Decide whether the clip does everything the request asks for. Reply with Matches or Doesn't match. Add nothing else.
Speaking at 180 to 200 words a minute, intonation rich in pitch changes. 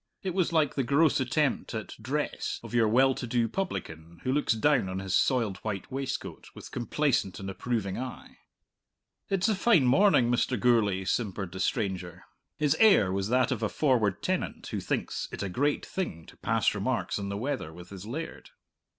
Matches